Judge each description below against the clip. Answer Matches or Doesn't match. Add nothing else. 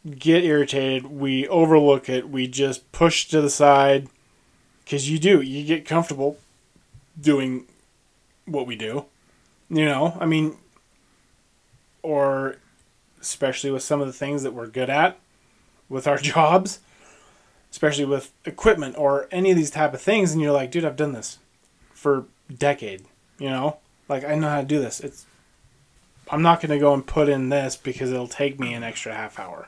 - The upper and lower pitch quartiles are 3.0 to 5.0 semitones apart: Doesn't match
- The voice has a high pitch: Doesn't match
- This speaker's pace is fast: Doesn't match